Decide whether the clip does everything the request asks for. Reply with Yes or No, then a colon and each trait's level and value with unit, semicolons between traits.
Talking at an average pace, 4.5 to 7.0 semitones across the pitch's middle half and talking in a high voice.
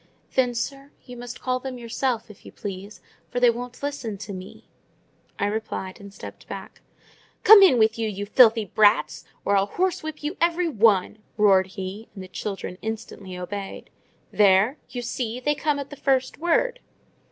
Yes: average, 165 wpm; average, 5.0 semitones; high, 230 Hz